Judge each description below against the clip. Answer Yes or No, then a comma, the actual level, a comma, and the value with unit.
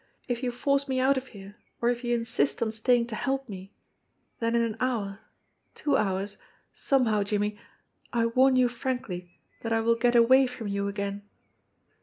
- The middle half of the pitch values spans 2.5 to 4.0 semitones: Yes, average, 3.6 semitones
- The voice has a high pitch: Yes, high, 230 Hz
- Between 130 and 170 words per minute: No, average, 180 wpm